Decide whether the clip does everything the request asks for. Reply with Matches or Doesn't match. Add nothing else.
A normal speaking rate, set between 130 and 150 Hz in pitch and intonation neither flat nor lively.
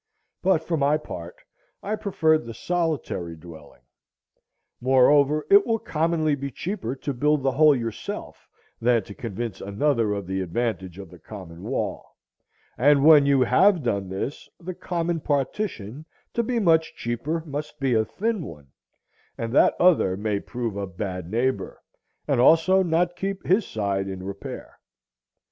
Doesn't match